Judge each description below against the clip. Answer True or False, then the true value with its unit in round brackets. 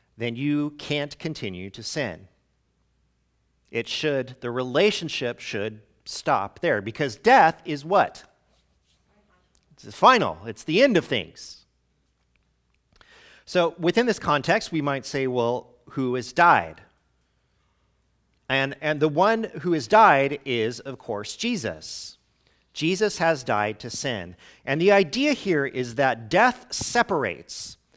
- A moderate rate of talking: False (130 wpm)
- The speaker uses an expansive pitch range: True (7.7 semitones)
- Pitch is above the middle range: False (135 Hz)